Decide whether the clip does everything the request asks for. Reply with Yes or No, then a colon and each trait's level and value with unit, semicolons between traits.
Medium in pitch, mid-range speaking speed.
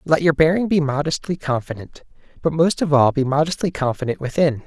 Yes: medium, 150 Hz; average, 180 wpm